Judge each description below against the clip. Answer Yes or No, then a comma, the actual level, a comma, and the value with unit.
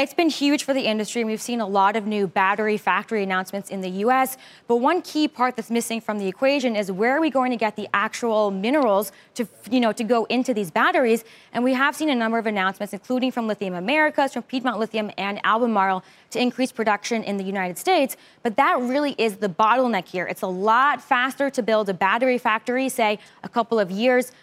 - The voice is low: No, high, 225 Hz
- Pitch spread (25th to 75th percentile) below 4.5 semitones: Yes, average, 3.9 semitones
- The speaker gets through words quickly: Yes, fast, 225 wpm